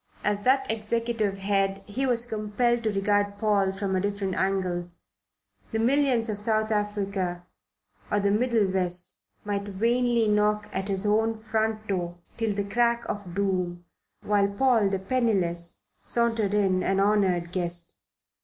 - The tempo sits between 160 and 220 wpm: No, average, 145 wpm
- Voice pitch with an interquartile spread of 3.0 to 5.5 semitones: No, narrow, 2.5 semitones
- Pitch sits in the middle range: No, high, 205 Hz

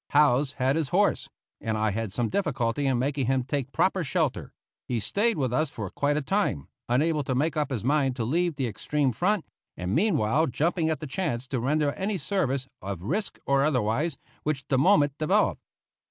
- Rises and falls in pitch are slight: No, average, 4.3 semitones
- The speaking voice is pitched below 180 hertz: Yes, medium, 140 Hz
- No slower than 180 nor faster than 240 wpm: Yes, average, 195 wpm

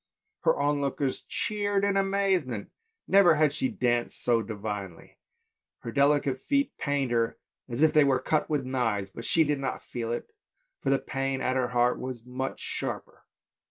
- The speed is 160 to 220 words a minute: Yes, average, 170 wpm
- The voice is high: No, low, 135 Hz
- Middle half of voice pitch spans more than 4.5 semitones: No, average, 4.2 semitones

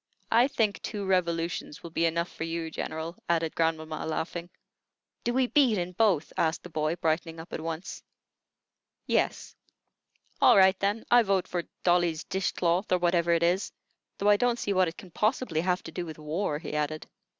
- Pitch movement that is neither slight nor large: Yes, average, 3.1 semitones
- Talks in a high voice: No, medium, 175 Hz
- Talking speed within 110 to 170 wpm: No, average, 185 wpm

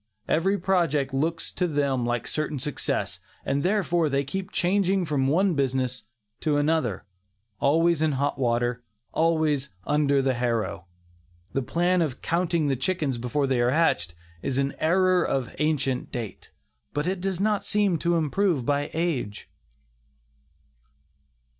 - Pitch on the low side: No, medium, 150 Hz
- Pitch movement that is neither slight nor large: Yes, average, 4.6 semitones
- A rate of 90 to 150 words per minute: Yes, average, 140 wpm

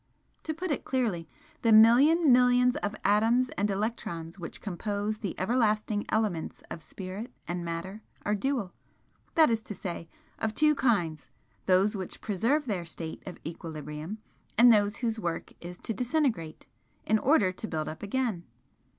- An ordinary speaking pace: Yes, average, 155 wpm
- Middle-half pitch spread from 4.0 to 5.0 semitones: No, wide, 5.4 semitones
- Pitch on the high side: Yes, high, 210 Hz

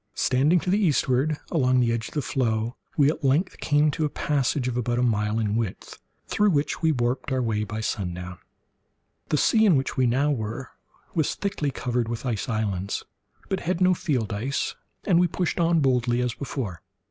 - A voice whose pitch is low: Yes, low, 130 Hz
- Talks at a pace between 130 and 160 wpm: No, average, 195 wpm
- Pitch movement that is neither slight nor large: Yes, average, 4.9 semitones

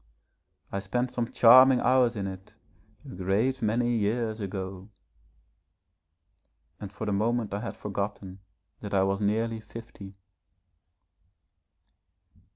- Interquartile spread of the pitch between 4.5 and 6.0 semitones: No, average, 3.2 semitones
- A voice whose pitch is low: Yes, low, 105 Hz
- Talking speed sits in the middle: No, slow, 120 wpm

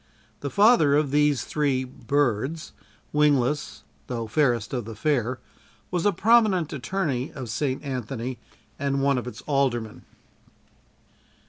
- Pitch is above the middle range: No, medium, 140 Hz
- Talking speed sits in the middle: No, slow, 125 wpm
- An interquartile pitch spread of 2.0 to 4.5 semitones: Yes, average, 3.4 semitones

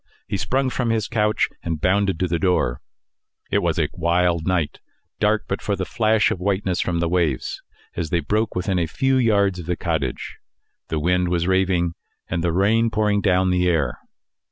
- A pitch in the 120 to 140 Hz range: No, very low, 90 Hz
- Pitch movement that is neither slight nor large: Yes, average, 3.5 semitones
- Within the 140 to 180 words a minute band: No, average, 190 wpm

